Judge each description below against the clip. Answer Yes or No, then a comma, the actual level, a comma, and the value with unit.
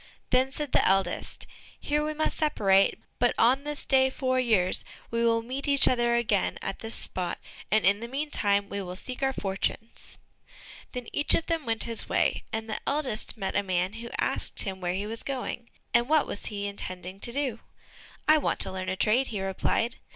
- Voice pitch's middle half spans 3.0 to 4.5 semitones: No, average, 5.0 semitones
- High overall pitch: Yes, high, 230 Hz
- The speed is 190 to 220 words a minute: Yes, average, 200 wpm